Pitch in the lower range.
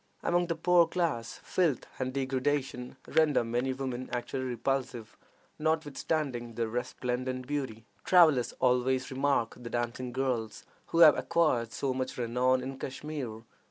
Yes: low, 130 Hz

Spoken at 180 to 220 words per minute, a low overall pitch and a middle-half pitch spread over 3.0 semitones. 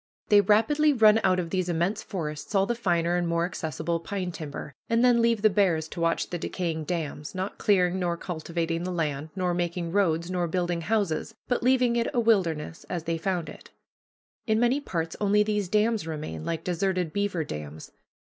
No: average, 190 wpm; medium, 180 Hz; average, 4.0 semitones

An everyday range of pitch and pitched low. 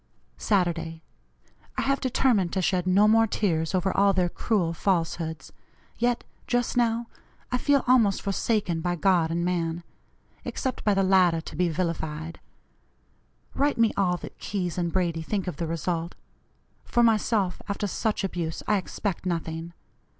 No: average, 4.0 semitones; medium, 185 Hz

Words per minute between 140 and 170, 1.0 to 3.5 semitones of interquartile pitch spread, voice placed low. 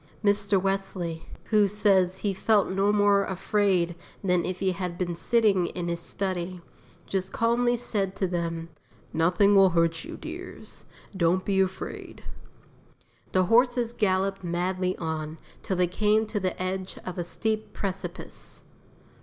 No: average, 145 wpm; narrow, 2.4 semitones; high, 190 Hz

